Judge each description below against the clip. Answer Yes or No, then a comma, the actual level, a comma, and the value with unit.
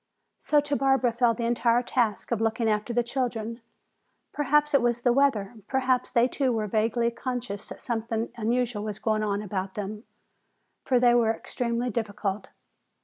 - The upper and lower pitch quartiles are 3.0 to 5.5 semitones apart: No, narrow, 2.4 semitones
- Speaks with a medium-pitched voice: No, high, 235 Hz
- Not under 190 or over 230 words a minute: No, average, 165 wpm